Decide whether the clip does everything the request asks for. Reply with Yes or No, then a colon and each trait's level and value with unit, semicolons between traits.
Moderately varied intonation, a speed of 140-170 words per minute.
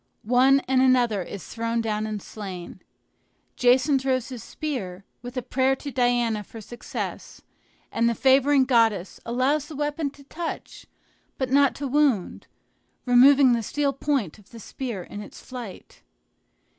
Yes: average, 3.4 semitones; average, 150 wpm